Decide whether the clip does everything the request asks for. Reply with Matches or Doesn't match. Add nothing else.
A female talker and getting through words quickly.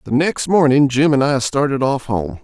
Doesn't match